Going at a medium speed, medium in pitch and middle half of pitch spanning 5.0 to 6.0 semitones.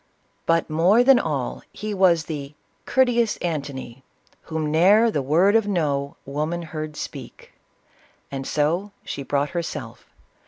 Yes: average, 145 wpm; medium, 160 Hz; wide, 5.4 semitones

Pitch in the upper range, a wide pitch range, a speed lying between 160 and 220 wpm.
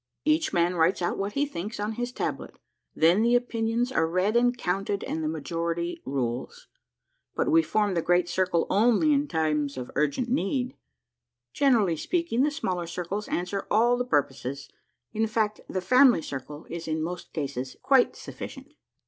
Yes: high, 195 Hz; wide, 6.7 semitones; average, 170 wpm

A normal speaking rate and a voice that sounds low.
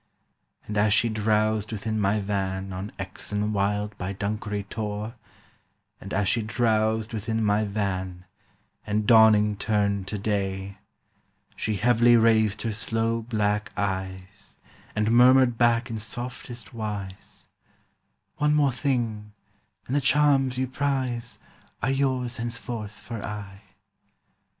No: slow, 125 wpm; low, 110 Hz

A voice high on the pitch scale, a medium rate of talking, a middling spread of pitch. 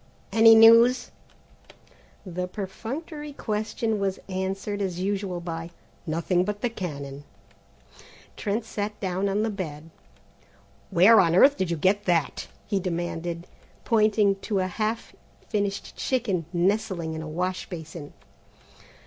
No: high, 195 Hz; slow, 125 wpm; average, 3.7 semitones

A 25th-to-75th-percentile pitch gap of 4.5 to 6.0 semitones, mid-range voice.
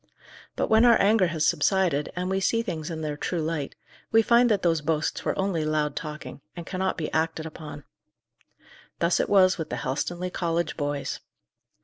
No: average, 3.7 semitones; medium, 165 Hz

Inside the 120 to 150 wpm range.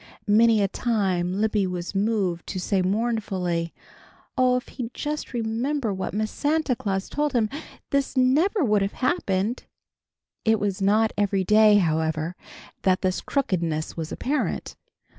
Yes: average, 140 wpm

